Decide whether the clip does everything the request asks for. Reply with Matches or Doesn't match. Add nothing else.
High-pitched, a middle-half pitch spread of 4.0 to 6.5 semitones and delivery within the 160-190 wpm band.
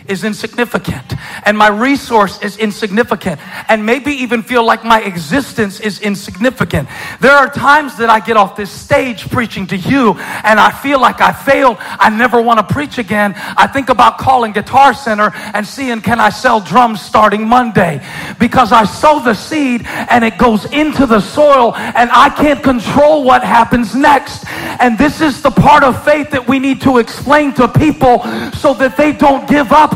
Matches